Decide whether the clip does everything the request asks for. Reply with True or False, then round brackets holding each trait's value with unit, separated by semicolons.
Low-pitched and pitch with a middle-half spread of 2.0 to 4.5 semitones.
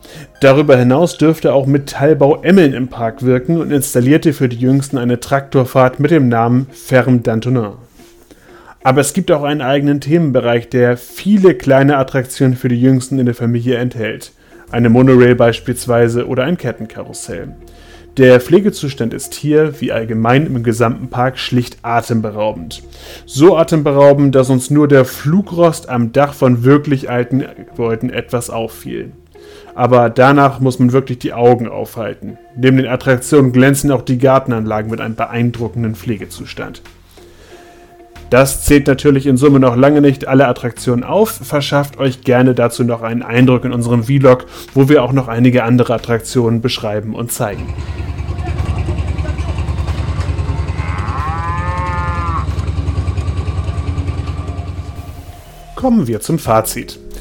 True (125 Hz; 3.5 semitones)